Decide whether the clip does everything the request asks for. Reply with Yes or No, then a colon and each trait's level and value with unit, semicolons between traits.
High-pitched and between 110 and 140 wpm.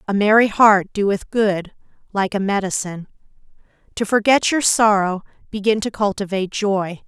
Yes: high, 205 Hz; slow, 135 wpm